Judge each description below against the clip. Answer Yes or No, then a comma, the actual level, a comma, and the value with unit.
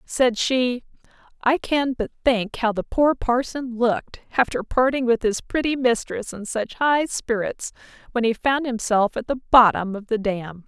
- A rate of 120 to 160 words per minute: No, average, 175 wpm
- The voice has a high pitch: Yes, high, 235 Hz